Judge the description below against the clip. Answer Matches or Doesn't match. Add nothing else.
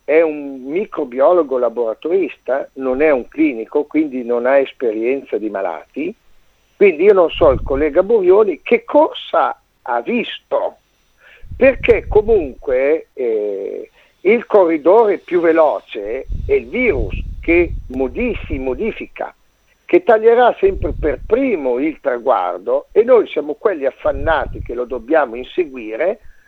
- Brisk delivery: Doesn't match